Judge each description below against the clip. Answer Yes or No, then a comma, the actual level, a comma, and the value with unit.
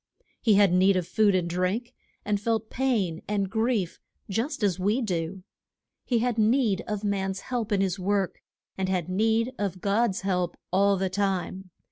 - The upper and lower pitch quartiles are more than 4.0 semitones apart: No, average, 3.0 semitones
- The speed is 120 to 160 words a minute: No, average, 170 wpm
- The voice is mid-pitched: No, high, 200 Hz